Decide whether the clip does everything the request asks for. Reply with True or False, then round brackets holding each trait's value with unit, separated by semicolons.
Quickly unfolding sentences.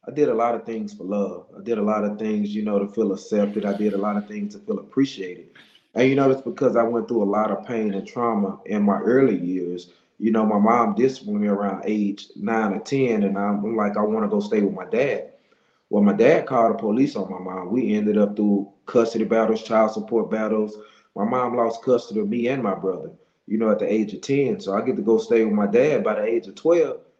True (255 wpm)